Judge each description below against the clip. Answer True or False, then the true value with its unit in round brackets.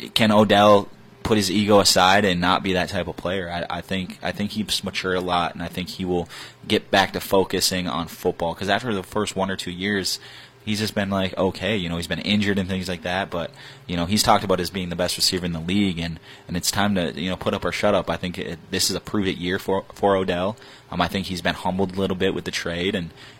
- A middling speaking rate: False (270 wpm)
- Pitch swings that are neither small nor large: False (2.2 semitones)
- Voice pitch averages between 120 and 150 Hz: False (95 Hz)